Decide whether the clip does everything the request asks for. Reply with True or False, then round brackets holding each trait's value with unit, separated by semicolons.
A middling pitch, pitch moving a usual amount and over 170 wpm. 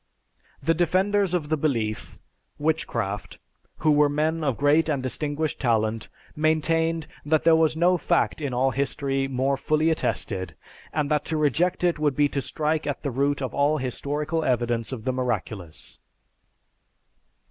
False (145 Hz; 3.4 semitones; 155 wpm)